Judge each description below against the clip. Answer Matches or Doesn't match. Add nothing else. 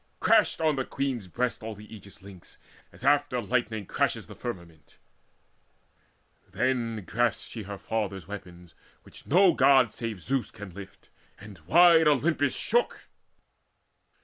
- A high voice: Doesn't match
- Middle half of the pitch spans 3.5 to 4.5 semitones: Doesn't match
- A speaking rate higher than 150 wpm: Doesn't match